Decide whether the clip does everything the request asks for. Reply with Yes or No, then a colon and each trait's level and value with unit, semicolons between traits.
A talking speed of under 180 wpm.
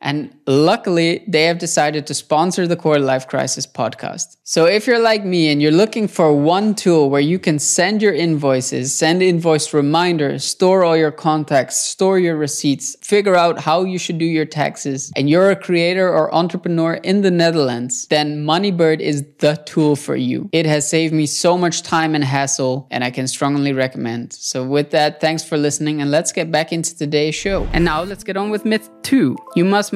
No: average, 200 wpm